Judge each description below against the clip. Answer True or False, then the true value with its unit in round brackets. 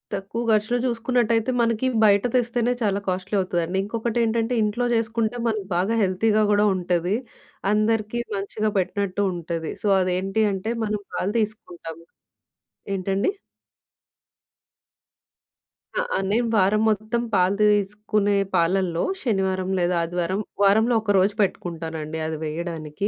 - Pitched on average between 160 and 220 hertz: True (205 Hz)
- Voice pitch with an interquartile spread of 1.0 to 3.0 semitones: False (3.4 semitones)